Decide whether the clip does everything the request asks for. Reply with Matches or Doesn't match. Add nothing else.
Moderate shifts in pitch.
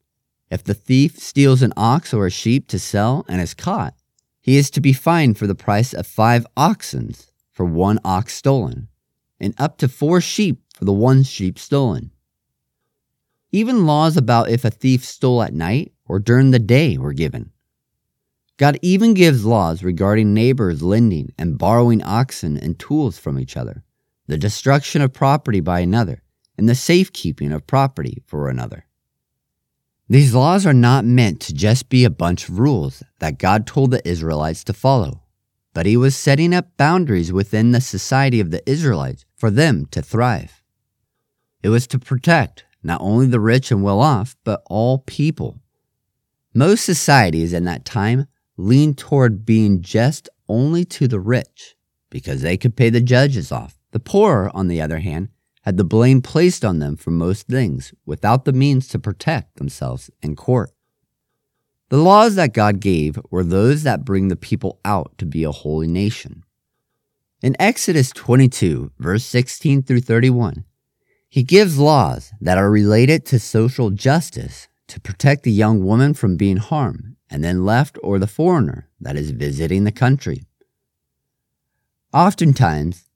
Doesn't match